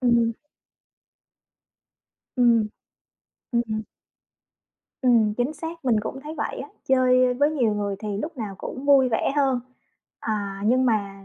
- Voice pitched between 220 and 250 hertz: Yes, high, 245 Hz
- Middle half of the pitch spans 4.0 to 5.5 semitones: No, average, 3.6 semitones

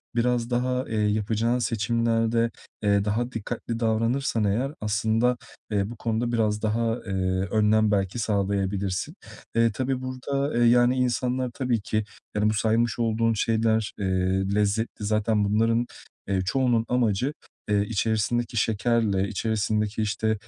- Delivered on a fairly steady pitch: Yes, narrow, 2.3 semitones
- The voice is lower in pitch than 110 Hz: No, low, 115 Hz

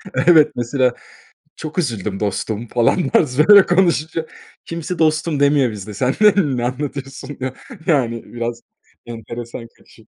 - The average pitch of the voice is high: No, low, 135 Hz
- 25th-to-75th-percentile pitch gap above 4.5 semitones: Yes, average, 4.9 semitones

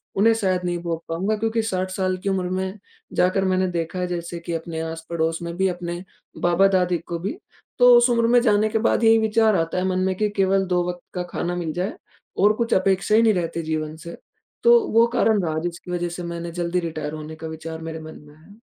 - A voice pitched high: No, medium, 180 Hz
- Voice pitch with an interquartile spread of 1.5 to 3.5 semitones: Yes, average, 3.1 semitones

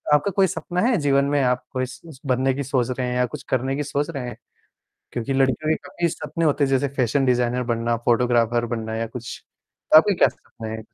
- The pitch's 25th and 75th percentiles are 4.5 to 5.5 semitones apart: No, average, 2.9 semitones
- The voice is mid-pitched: No, low, 130 Hz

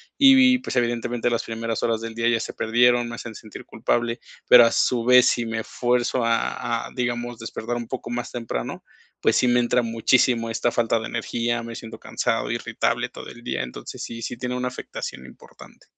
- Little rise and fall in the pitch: Yes, narrow, 1.1 semitones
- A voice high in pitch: No, low, 120 Hz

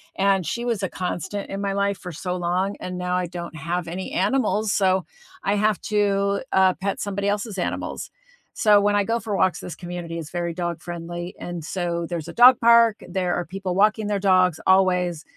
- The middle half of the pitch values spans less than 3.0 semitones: Yes, narrow, 2.4 semitones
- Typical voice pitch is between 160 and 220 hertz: Yes, high, 190 Hz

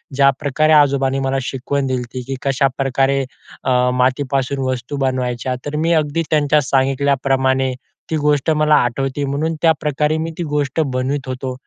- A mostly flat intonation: Yes, narrow, 2.1 semitones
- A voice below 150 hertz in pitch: Yes, low, 135 Hz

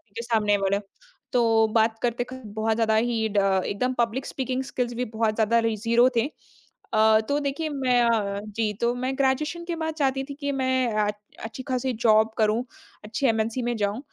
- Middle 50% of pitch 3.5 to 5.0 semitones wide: No, average, 3.0 semitones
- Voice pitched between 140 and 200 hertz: No, high, 235 Hz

